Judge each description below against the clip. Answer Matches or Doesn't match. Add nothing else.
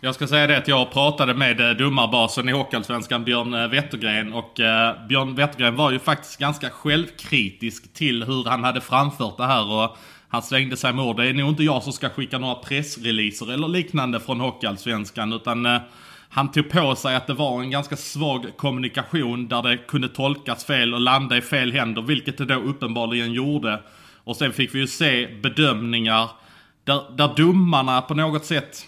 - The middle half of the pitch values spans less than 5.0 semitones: Matches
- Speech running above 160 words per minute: Matches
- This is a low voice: Matches